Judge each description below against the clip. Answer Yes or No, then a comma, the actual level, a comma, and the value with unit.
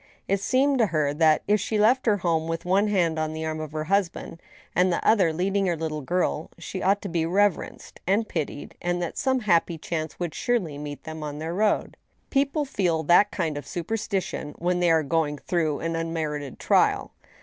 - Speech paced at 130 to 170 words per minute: No, average, 200 wpm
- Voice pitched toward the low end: No, medium, 170 Hz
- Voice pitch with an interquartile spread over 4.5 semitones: No, average, 4.1 semitones